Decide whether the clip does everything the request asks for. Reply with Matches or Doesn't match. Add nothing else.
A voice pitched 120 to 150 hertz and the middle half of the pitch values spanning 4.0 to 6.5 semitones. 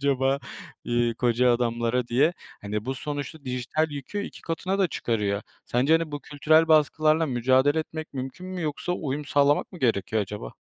Matches